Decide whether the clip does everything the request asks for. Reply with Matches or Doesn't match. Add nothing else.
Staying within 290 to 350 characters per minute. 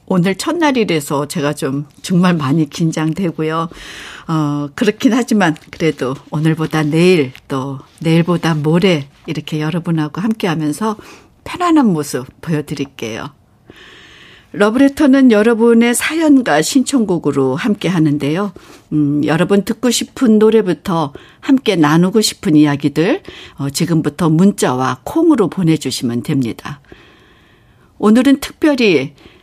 Doesn't match